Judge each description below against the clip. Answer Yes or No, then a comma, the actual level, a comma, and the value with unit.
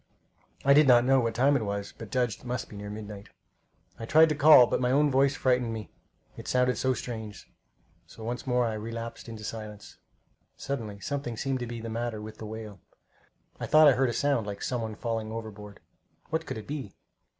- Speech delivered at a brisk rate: Yes, fast, 210 wpm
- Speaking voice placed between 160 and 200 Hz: No, low, 115 Hz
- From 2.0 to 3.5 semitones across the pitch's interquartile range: Yes, average, 3.2 semitones